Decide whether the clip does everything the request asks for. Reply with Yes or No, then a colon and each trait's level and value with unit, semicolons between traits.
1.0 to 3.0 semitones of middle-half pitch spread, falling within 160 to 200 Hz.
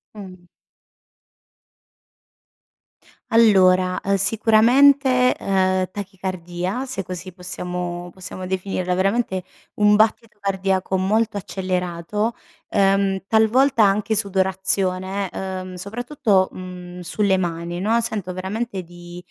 Yes: narrow, 2.5 semitones; high, 190 Hz